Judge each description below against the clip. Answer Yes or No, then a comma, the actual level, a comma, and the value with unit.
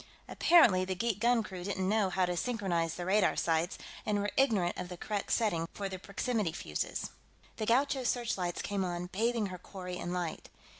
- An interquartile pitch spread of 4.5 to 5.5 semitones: No, average, 3.7 semitones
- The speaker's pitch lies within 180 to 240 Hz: Yes, high, 190 Hz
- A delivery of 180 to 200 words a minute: Yes, average, 185 wpm